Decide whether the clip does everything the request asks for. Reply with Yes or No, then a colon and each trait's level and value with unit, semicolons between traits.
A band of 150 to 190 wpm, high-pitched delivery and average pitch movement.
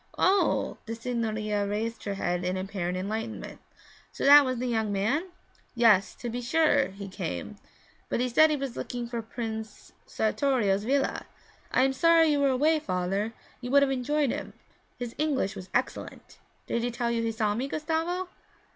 Yes: average, 175 wpm; high, 235 Hz; average, 4.7 semitones